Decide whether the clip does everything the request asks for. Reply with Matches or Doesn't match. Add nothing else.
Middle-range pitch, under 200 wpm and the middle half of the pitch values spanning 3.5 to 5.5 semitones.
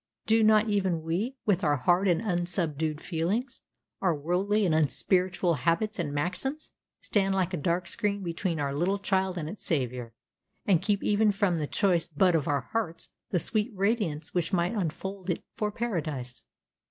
Matches